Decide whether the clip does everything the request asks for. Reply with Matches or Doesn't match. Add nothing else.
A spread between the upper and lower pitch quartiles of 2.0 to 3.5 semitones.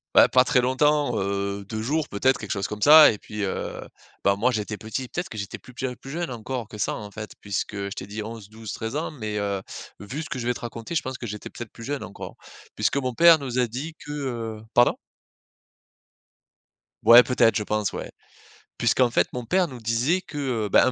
Doesn't match